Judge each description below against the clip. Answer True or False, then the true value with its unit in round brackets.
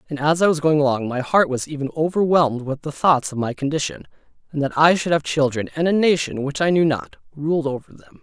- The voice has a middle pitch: True (150 Hz)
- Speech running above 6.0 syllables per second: False (5.9 syllables/s)